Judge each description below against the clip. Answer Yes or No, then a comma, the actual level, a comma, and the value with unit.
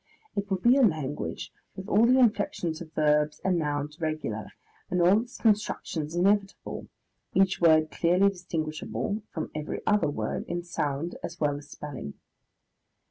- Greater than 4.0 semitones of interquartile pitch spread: Yes, average, 4.7 semitones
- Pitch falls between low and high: Yes, medium, 170 Hz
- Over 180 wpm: No, average, 150 wpm